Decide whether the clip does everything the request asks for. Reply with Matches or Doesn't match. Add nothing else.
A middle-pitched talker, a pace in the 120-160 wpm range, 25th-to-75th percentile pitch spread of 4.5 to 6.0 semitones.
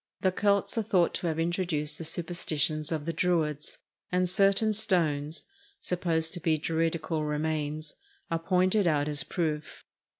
Doesn't match